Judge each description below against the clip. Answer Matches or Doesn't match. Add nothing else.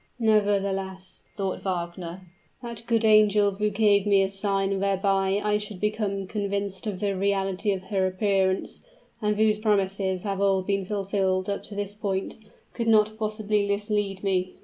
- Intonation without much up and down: Matches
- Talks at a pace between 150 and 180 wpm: Matches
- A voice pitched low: Doesn't match